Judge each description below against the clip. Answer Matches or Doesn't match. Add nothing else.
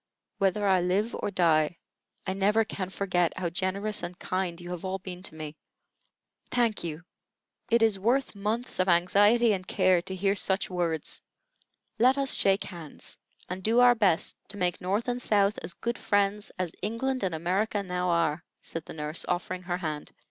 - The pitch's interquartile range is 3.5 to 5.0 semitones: Doesn't match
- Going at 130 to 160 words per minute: Doesn't match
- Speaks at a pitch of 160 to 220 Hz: Matches